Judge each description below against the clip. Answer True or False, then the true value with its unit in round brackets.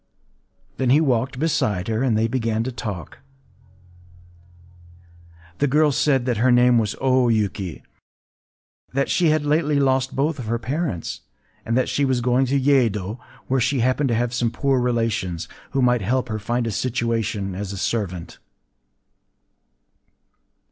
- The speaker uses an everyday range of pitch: True (3.1 semitones)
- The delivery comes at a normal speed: True (160 wpm)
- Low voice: True (125 Hz)